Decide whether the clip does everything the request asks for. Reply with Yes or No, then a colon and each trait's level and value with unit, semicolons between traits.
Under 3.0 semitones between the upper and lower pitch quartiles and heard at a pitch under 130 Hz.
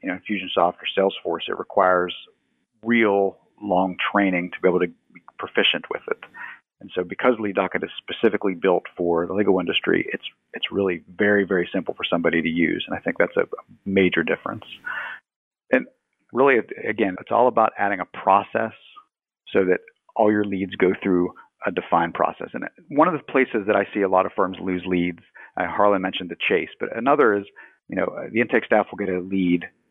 Yes: narrow, 2.4 semitones; very low, 95 Hz